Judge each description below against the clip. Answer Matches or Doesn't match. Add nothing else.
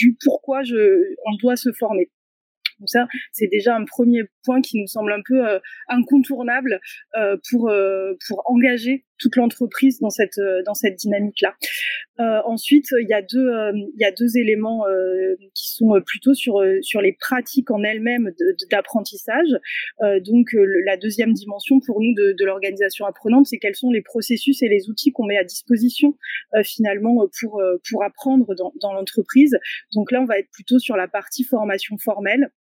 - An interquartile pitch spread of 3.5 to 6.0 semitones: Matches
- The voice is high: Matches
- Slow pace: Doesn't match